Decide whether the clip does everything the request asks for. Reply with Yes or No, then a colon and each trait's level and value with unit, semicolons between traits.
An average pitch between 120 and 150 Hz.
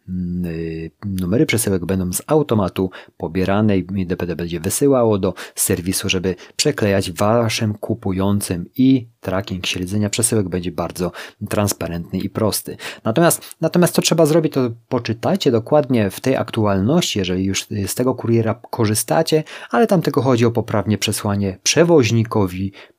No: low, 105 Hz